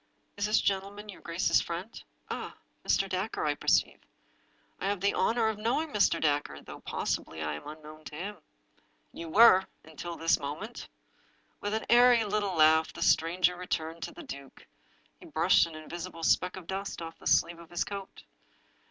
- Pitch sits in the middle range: Yes, medium, 180 Hz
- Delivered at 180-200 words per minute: Yes, average, 185 wpm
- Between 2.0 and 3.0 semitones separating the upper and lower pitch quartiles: No, average, 4.2 semitones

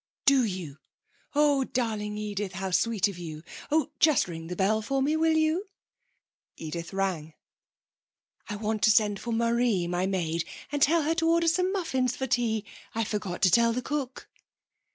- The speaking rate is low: No, average, 175 wpm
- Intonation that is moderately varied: No, wide, 6.5 semitones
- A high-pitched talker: Yes, high, 220 Hz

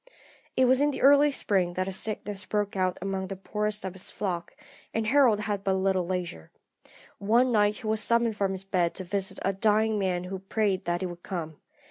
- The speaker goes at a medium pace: No, fast, 210 wpm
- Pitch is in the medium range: No, high, 195 Hz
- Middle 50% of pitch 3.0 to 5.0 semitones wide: No, narrow, 2.6 semitones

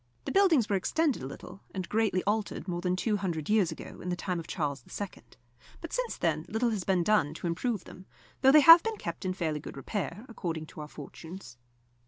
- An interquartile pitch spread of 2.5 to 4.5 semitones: No, average, 4.9 semitones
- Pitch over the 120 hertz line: Yes, medium, 185 Hz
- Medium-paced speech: No, fast, 220 wpm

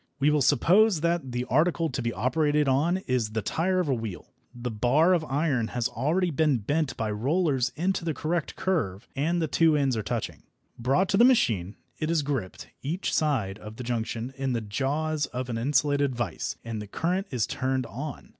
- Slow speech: No, average, 200 wpm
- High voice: No, medium, 140 Hz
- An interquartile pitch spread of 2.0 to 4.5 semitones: No, average, 5.2 semitones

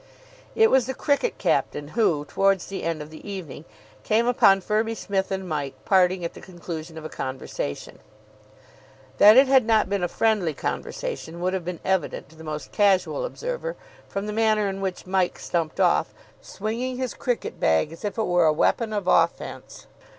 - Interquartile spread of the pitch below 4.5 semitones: No, average, 5.0 semitones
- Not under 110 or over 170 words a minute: No, average, 185 wpm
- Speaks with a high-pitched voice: Yes, high, 195 Hz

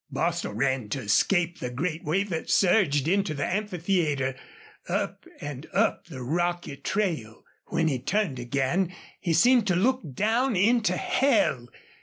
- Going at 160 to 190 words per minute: No, average, 145 wpm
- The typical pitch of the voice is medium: Yes, medium, 170 Hz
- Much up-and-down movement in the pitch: Yes, wide, 6.2 semitones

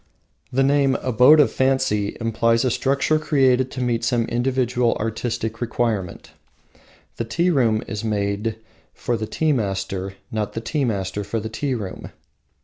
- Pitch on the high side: No, low, 115 Hz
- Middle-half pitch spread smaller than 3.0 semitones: No, average, 3.4 semitones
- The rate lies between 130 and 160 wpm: Yes, average, 150 wpm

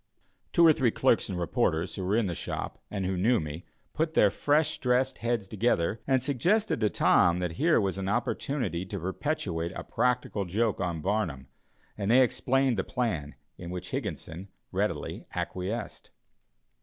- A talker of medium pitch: No, low, 105 Hz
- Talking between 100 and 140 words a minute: No, average, 170 wpm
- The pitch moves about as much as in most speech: No, wide, 5.8 semitones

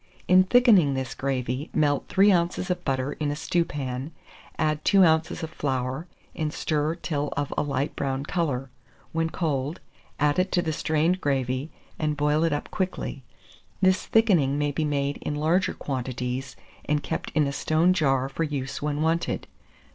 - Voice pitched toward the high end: No, medium, 150 Hz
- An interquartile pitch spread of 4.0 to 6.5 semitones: No, average, 3.3 semitones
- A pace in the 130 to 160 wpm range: No, average, 170 wpm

